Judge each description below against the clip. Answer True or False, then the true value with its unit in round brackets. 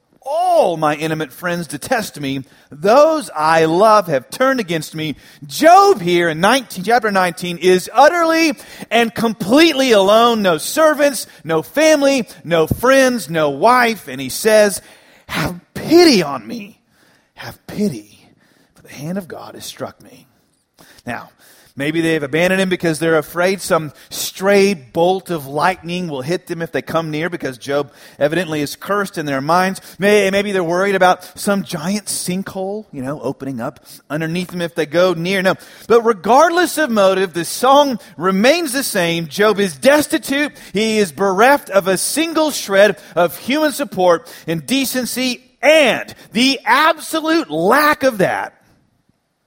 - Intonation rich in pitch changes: True (7.4 semitones)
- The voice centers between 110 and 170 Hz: False (190 Hz)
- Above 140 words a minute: True (150 wpm)